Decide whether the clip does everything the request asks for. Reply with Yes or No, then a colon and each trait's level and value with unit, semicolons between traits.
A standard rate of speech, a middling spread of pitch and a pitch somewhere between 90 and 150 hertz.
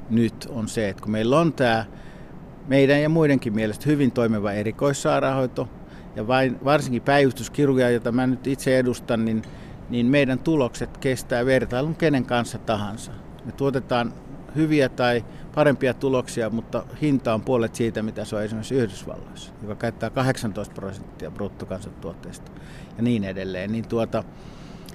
Yes: average, 140 wpm; average, 3.5 semitones; low, 120 Hz